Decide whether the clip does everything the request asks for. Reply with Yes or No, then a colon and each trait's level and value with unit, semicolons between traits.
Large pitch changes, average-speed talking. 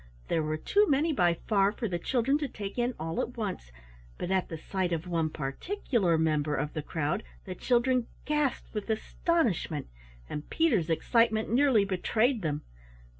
Yes: wide, 7.3 semitones; average, 170 wpm